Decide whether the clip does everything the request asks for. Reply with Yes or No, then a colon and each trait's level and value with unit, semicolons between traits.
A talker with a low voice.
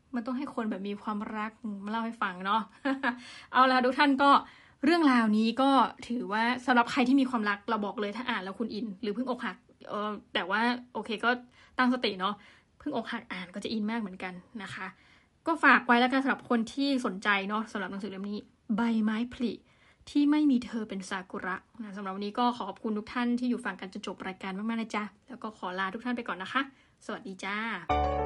No: high, 225 Hz